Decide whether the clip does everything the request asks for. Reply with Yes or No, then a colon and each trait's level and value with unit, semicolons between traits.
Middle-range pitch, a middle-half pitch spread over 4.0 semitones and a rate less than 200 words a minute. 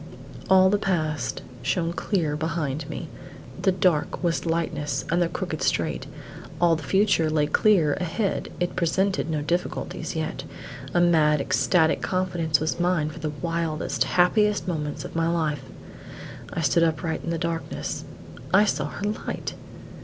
No: medium, 165 Hz; average, 2.7 semitones; average, 150 wpm